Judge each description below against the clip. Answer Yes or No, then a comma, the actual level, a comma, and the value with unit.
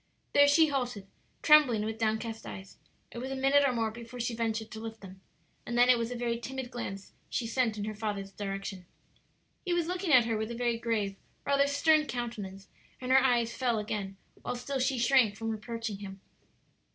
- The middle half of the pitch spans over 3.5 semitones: No, average, 3.2 semitones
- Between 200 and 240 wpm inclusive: Yes, fast, 205 wpm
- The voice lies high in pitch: Yes, high, 235 Hz